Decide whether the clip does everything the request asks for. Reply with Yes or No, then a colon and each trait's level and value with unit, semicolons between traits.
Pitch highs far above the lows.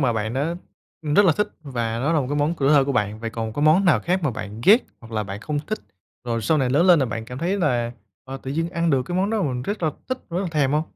Yes: wide, 6.1 semitones